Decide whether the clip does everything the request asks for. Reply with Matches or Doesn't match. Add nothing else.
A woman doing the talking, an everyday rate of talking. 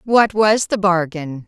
Matches